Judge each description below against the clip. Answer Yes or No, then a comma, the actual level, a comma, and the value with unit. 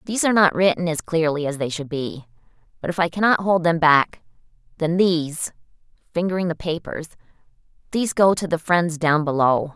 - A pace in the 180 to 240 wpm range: No, average, 165 wpm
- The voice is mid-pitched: Yes, medium, 165 Hz